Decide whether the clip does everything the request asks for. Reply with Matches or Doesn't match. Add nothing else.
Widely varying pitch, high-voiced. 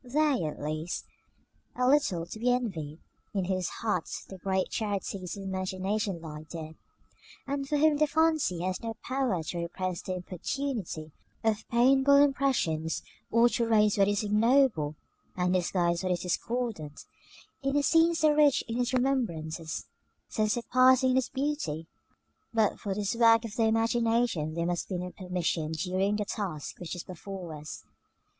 Matches